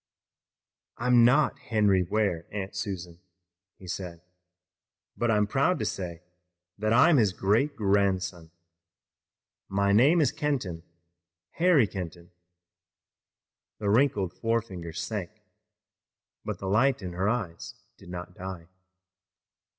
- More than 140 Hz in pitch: No, low, 100 Hz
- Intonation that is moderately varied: Yes, average, 4.8 semitones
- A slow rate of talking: Yes, slow, 110 wpm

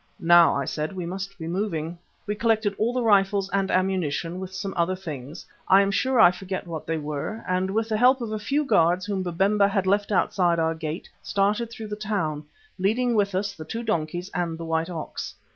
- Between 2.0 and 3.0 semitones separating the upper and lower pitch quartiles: No, average, 3.7 semitones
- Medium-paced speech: No, fast, 210 wpm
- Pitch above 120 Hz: Yes, high, 190 Hz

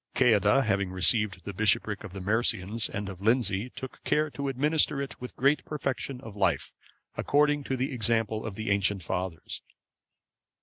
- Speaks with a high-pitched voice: No, low, 110 Hz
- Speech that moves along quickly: No, average, 165 wpm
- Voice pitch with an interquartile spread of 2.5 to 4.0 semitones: No, average, 5.1 semitones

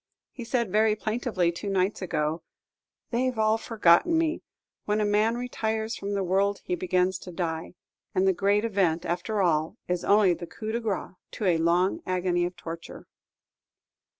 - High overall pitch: Yes, high, 195 Hz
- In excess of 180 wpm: No, average, 175 wpm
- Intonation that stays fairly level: No, average, 3.8 semitones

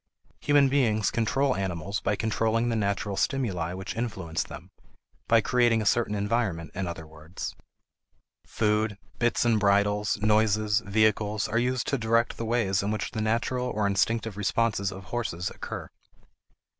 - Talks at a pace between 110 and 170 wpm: Yes, average, 150 wpm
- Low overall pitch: Yes, low, 110 Hz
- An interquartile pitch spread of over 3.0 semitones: No, average, 2.7 semitones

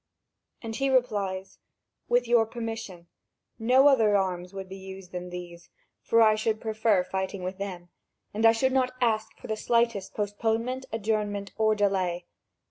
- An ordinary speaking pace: Yes, average, 160 wpm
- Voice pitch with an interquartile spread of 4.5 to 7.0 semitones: No, average, 3.1 semitones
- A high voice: Yes, high, 215 Hz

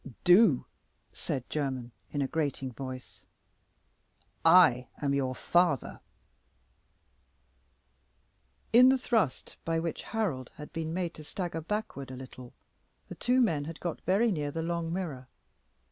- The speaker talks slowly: Yes, slow, 130 wpm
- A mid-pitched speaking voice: Yes, medium, 160 Hz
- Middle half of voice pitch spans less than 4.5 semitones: No, average, 5.1 semitones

